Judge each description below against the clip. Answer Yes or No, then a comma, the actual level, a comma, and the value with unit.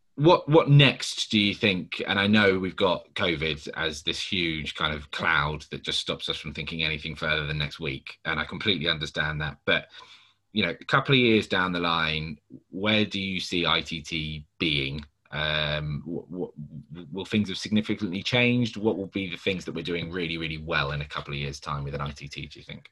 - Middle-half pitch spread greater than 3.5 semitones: Yes, average, 4.5 semitones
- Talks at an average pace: No, fast, 210 wpm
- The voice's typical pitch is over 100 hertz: No, very low, 80 Hz